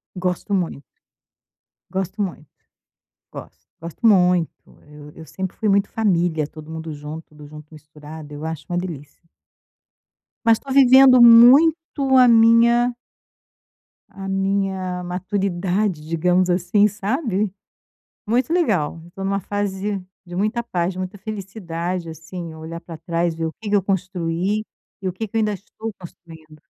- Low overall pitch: No, medium, 185 Hz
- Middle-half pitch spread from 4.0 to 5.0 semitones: Yes, average, 4.3 semitones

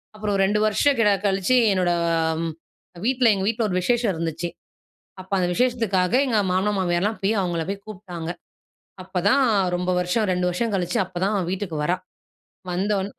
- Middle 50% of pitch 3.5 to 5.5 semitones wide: No, average, 3.1 semitones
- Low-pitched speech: No, high, 190 Hz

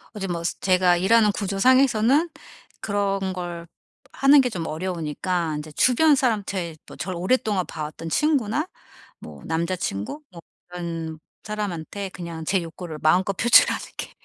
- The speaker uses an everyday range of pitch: Yes, average, 4.2 semitones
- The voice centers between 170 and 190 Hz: Yes, medium, 185 Hz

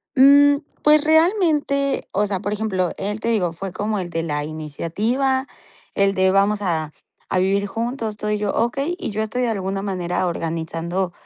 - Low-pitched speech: No, high, 205 Hz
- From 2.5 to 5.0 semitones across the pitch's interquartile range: No, wide, 5.4 semitones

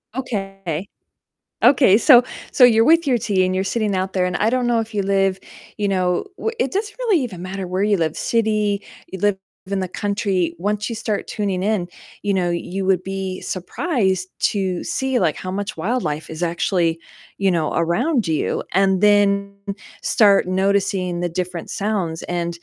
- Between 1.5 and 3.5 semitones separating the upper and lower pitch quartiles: Yes, average, 2.8 semitones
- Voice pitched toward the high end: Yes, high, 195 Hz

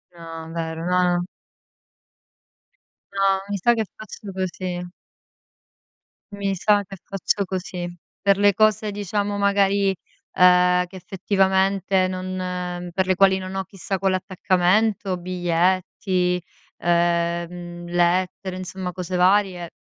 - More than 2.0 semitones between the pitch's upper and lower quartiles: No, narrow, 1.7 semitones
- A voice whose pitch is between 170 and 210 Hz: Yes, medium, 185 Hz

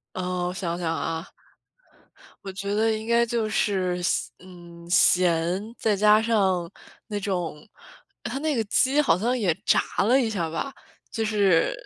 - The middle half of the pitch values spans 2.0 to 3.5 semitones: No, average, 4.0 semitones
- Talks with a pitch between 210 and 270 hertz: No, high, 195 Hz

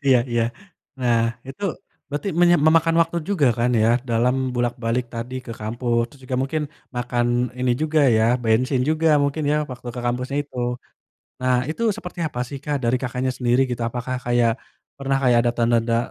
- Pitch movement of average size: Yes, average, 3.0 semitones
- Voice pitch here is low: Yes, low, 125 Hz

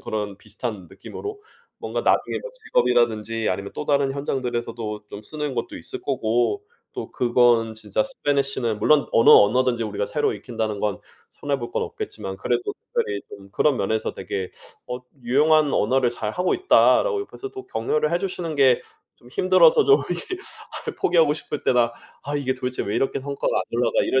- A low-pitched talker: Yes, low, 125 Hz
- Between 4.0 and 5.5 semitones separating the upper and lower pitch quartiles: Yes, average, 5.1 semitones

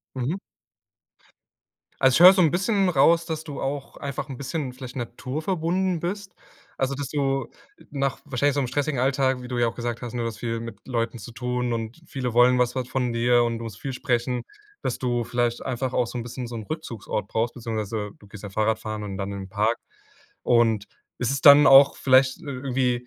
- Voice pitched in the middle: No, low, 125 Hz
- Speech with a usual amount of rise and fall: Yes, average, 3.0 semitones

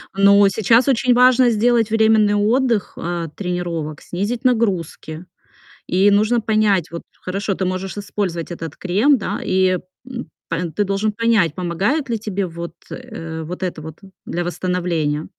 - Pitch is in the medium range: No, high, 195 Hz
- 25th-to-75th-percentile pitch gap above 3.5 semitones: Yes, average, 4.3 semitones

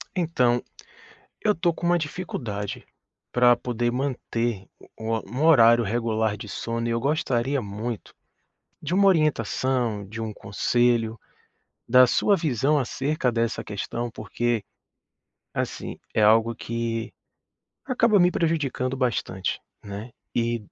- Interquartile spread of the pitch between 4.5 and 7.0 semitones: No, average, 3.8 semitones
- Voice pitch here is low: Yes, low, 120 Hz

